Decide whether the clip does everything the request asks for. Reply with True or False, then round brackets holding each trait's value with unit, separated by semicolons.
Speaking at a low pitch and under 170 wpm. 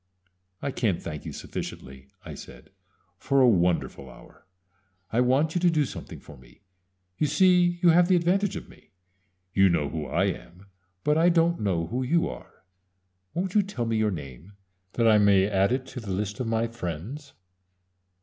False (115 Hz; 185 wpm)